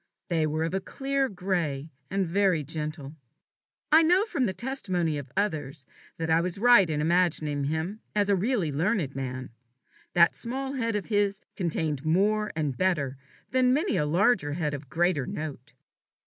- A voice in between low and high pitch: Yes, medium, 175 Hz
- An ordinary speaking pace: Yes, average, 160 wpm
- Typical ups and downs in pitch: No, wide, 5.7 semitones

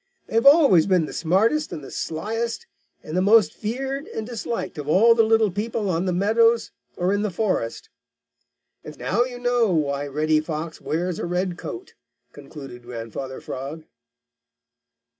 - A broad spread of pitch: Yes, wide, 6.5 semitones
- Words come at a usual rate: Yes, average, 160 wpm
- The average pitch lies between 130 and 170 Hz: No, high, 190 Hz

